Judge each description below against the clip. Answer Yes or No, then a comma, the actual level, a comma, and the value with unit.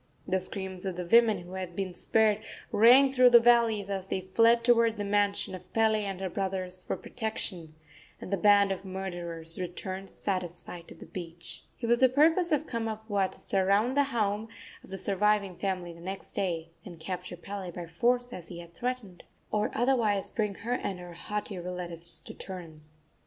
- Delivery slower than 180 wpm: No, average, 185 wpm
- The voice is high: Yes, high, 195 Hz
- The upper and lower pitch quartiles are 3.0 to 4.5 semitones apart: Yes, average, 3.7 semitones